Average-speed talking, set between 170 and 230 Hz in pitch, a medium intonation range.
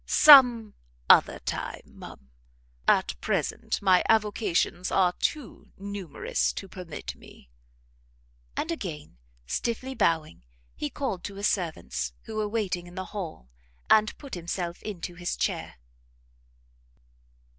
No: slow, 120 wpm; high, 190 Hz; average, 4.2 semitones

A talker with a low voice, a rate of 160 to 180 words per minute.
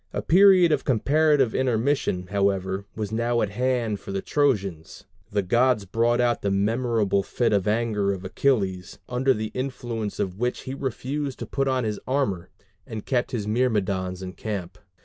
Yes: low, 115 Hz; average, 170 wpm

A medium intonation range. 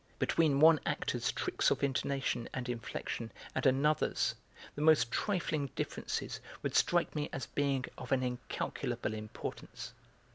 Yes: average, 3.4 semitones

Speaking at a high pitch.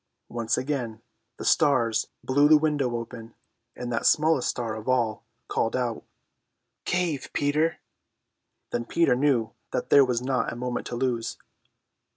No: low, 125 Hz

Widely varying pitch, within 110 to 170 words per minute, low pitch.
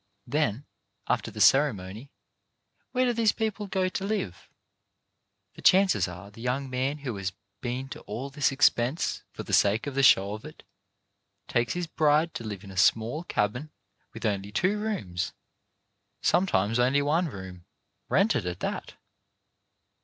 Yes: wide, 7.7 semitones; average, 160 wpm; low, 130 Hz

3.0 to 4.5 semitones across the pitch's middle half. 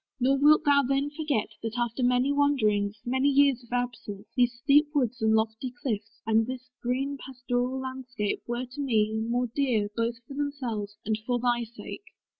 Yes: average, 3.4 semitones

